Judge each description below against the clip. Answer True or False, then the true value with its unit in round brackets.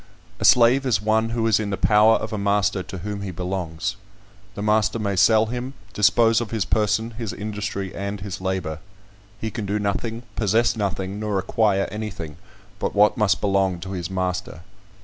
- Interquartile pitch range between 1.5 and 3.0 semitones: True (2.5 semitones)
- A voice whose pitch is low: True (105 Hz)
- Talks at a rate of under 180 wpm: False (185 wpm)